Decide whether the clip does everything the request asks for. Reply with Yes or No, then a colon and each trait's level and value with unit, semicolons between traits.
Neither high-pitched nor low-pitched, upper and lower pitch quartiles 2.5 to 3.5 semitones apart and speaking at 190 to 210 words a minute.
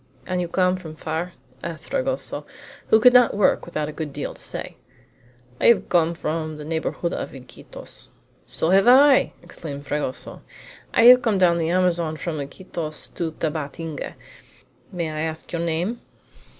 No: medium, 170 Hz; average, 3.0 semitones; average, 165 wpm